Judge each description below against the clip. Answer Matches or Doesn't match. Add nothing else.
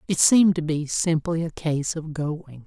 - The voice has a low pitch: Doesn't match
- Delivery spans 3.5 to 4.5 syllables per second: Matches